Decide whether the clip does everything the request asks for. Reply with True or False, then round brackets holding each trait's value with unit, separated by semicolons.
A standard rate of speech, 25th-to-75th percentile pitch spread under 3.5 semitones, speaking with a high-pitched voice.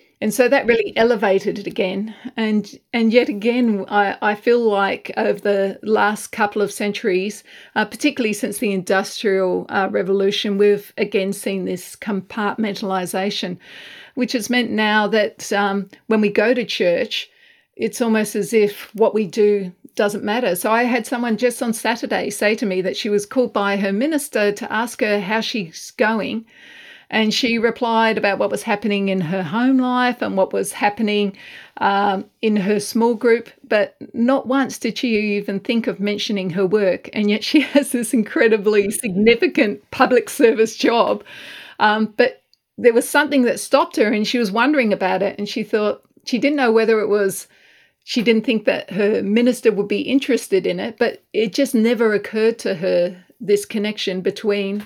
True (175 wpm; 2.9 semitones; 220 Hz)